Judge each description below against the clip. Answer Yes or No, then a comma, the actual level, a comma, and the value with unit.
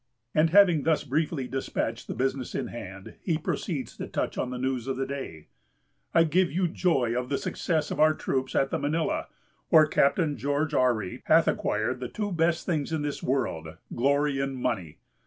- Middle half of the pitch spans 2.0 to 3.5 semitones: No, average, 3.9 semitones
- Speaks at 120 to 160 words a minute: No, average, 190 wpm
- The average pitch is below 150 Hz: Yes, medium, 140 Hz